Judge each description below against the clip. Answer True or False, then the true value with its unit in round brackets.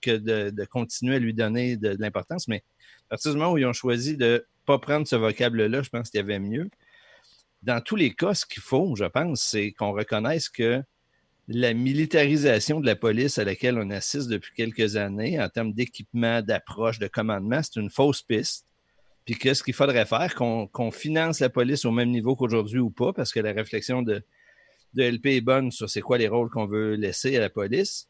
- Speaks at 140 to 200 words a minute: False (220 wpm)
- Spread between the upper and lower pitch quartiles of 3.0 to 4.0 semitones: True (3.3 semitones)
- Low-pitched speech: True (120 Hz)